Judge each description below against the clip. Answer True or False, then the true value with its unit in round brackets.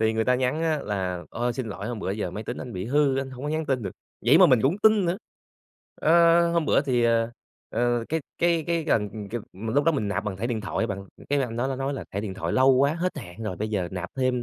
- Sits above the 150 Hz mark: False (120 Hz)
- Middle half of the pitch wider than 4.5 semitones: True (5.5 semitones)